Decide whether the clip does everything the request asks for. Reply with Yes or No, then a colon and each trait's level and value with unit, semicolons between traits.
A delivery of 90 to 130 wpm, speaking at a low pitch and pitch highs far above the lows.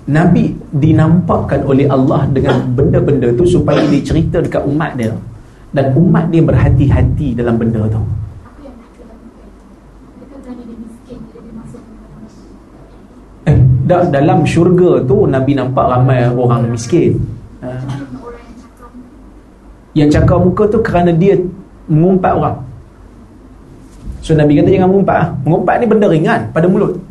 No: average, 110 wpm; medium, 150 Hz; wide, 5.7 semitones